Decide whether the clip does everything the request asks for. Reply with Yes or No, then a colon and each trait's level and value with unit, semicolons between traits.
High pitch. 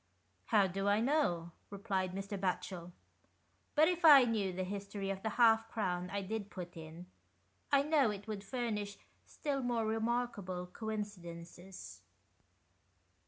Yes: high, 205 Hz